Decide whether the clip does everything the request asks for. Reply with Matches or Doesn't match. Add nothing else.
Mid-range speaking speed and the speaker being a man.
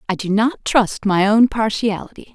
Doesn't match